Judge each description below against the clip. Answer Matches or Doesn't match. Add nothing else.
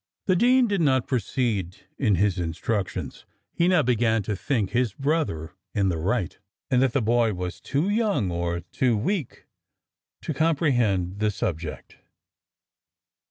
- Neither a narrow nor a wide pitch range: Doesn't match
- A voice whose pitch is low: Matches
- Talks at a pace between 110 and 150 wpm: Matches